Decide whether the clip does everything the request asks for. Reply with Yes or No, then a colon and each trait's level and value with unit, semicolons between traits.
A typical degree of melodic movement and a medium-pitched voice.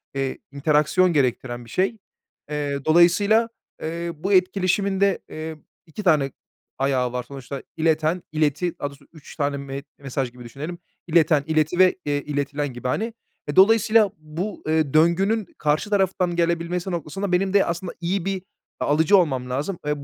Yes: average, 4.5 semitones; medium, 160 Hz